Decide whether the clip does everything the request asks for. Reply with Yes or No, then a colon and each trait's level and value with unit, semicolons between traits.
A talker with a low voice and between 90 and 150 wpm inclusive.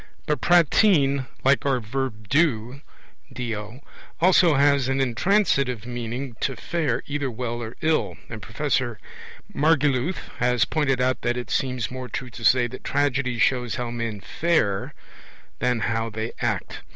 Yes: low, 130 Hz; average, 140 wpm